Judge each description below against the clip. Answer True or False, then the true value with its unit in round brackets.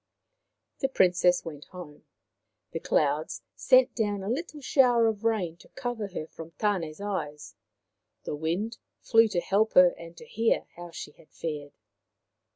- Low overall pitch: False (185 Hz)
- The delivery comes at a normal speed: True (160 wpm)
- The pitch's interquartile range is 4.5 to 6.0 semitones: True (5.6 semitones)